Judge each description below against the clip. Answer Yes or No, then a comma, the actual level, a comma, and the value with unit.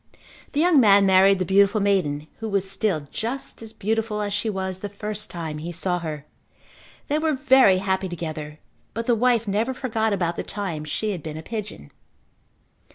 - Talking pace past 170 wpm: Yes, average, 185 wpm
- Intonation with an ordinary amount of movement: Yes, average, 4.1 semitones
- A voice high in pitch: Yes, high, 200 Hz